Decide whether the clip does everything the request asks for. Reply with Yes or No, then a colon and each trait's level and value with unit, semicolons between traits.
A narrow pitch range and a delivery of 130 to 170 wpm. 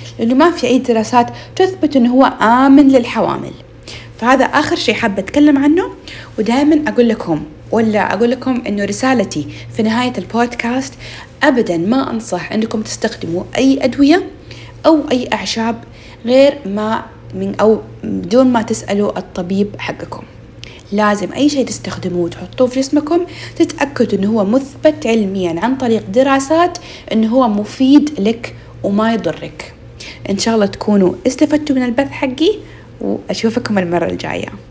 No: average, 4.8 semitones; fast, 135 wpm